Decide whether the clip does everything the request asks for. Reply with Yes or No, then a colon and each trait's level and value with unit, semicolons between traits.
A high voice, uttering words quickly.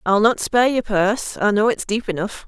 Yes: high, 215 Hz; fast, 220 wpm